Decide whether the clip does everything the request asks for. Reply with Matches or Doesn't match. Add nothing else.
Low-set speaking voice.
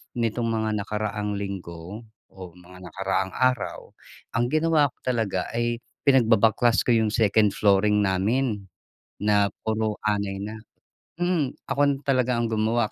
Matches